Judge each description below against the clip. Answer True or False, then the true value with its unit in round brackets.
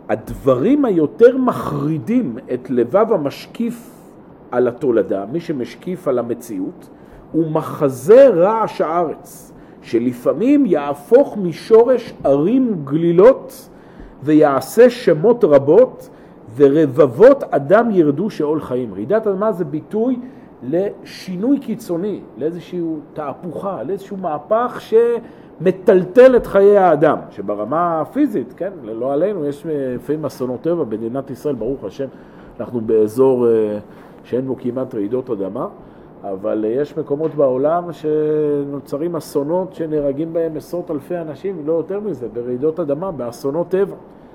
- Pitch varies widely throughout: True (7.2 semitones)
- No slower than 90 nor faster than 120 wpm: True (110 wpm)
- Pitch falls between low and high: True (160 Hz)